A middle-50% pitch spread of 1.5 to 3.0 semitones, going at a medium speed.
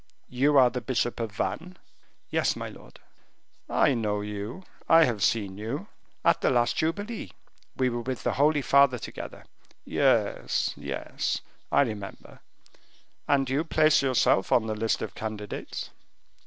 No: average, 4.7 semitones; average, 145 wpm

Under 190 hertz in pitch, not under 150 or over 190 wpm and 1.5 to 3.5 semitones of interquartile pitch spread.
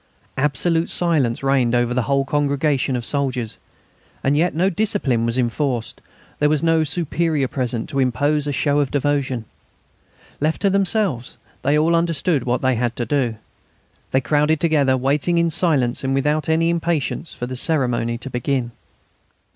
No: medium, 140 Hz; average, 160 wpm; average, 4.0 semitones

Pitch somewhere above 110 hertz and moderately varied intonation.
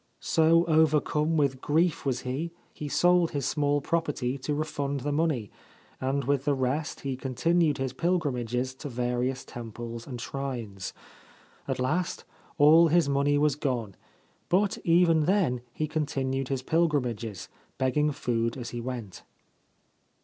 Yes: medium, 140 Hz; average, 3.8 semitones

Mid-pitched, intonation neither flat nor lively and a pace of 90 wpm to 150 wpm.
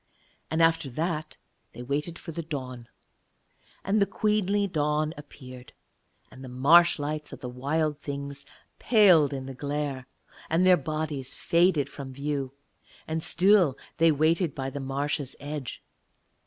Yes: medium, 150 Hz; average, 3.3 semitones; average, 140 wpm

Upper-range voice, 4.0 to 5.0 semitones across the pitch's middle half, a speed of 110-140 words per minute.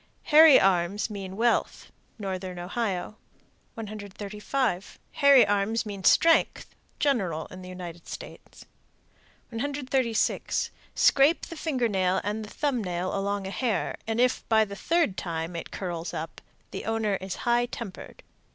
Yes: high, 210 Hz; average, 4.5 semitones; slow, 135 wpm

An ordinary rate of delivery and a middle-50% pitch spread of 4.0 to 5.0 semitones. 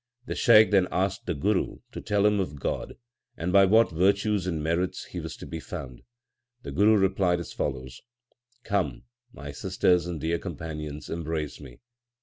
Yes: average, 170 wpm; average, 4.4 semitones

